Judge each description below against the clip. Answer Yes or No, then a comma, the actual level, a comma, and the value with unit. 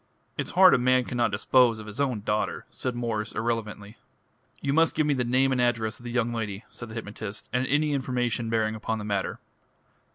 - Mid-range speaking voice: No, low, 120 Hz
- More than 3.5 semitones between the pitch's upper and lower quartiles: No, average, 2.7 semitones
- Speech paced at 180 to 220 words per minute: Yes, fast, 205 wpm